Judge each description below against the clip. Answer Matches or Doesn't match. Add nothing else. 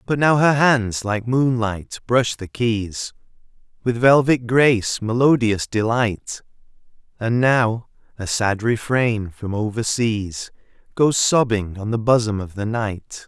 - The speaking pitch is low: Matches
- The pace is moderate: Doesn't match